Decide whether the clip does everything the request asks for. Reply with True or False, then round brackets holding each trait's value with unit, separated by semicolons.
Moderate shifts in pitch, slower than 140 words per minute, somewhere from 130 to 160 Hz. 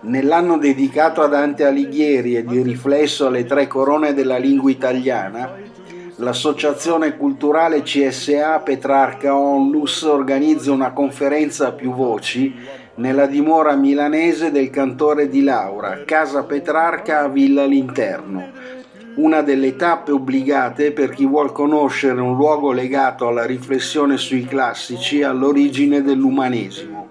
False (2.0 semitones; 120 wpm; 140 Hz)